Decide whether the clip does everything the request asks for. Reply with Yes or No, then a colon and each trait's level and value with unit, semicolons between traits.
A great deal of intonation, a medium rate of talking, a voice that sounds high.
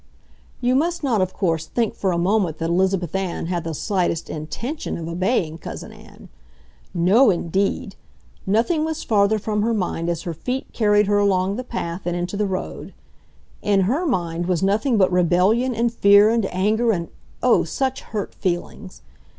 No: average, 4.4 semitones; average, 175 wpm; high, 195 Hz